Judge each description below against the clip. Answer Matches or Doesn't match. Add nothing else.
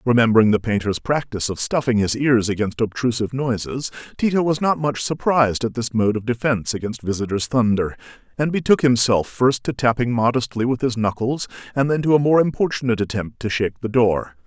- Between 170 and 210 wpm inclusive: Matches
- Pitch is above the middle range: Doesn't match